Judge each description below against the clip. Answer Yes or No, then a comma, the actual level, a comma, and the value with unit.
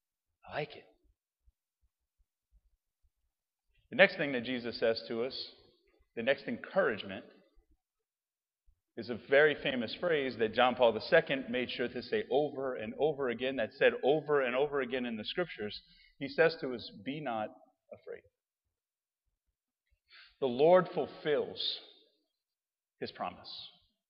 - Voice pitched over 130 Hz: Yes, medium, 140 Hz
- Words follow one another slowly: Yes, slow, 130 wpm